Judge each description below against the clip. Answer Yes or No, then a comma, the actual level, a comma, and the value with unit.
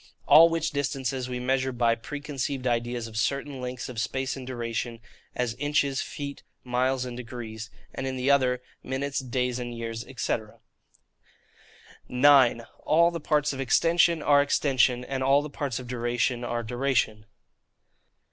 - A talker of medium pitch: No, low, 130 Hz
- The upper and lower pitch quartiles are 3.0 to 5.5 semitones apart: No, narrow, 2.6 semitones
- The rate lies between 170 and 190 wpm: No, average, 145 wpm